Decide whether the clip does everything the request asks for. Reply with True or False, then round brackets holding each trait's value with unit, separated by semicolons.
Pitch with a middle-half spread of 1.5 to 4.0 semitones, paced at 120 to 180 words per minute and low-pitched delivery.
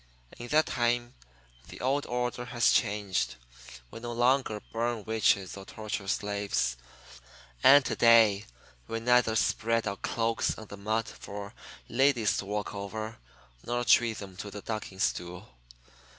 True (2.9 semitones; 145 wpm; 110 Hz)